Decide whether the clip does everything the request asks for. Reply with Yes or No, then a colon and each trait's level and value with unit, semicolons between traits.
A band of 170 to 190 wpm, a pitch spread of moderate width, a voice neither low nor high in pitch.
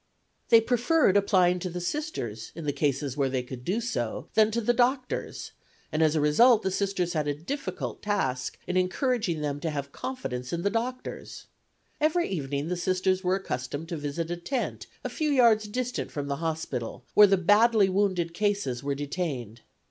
No: average, 180 wpm; wide, 7.2 semitones; medium, 180 Hz